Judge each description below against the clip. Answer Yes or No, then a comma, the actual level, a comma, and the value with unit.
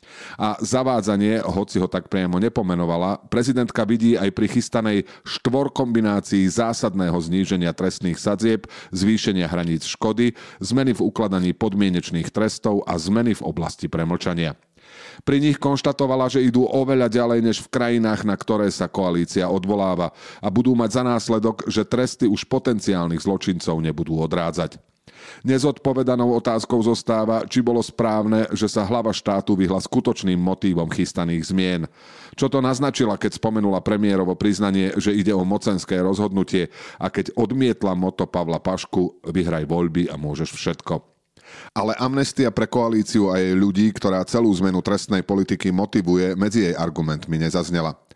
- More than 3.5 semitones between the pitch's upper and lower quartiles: Yes, average, 4.2 semitones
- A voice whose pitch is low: Yes, low, 105 Hz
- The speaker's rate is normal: Yes, average, 140 wpm